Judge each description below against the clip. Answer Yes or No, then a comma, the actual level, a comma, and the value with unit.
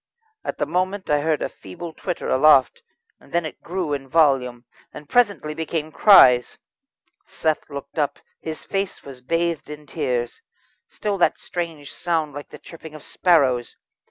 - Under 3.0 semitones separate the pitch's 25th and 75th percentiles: No, average, 3.5 semitones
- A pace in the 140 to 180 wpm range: Yes, average, 155 wpm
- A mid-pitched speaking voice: Yes, medium, 155 Hz